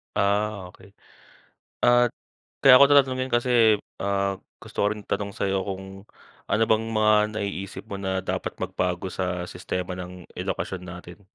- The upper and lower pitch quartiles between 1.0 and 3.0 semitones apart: Yes, narrow, 2.6 semitones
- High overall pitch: No, low, 100 Hz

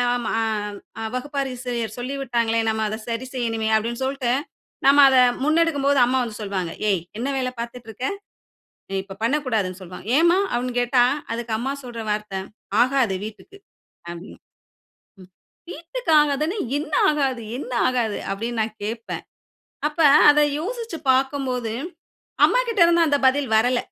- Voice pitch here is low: No, very high, 250 Hz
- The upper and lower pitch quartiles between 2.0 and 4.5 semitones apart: Yes, average, 4.0 semitones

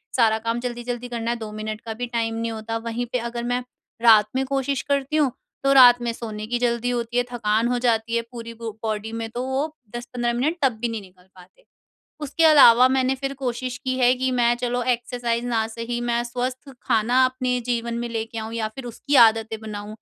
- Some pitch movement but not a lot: No, narrow, 1.7 semitones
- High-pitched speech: Yes, high, 240 Hz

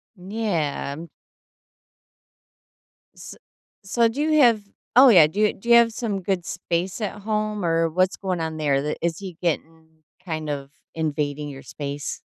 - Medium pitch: Yes, medium, 175 Hz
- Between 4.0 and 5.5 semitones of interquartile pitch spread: Yes, average, 5.2 semitones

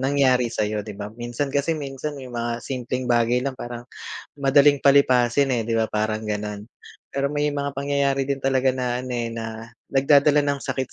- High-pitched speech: No, low, 130 Hz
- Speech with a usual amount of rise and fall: Yes, average, 3.0 semitones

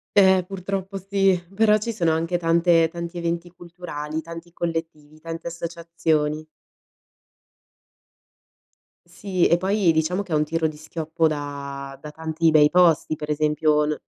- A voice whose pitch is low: No, medium, 165 Hz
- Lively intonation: No, narrow, 2.5 semitones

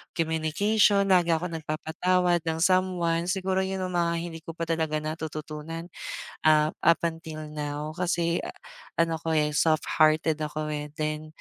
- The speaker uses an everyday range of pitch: No, narrow, 2.1 semitones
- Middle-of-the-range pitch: Yes, medium, 165 Hz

